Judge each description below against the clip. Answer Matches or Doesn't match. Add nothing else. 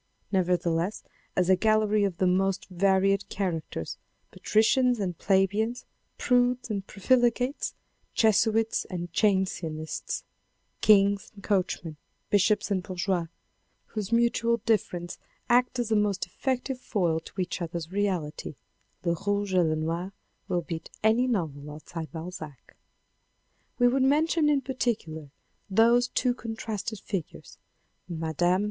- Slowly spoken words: Matches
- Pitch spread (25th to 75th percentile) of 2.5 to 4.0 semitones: Doesn't match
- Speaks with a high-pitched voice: Matches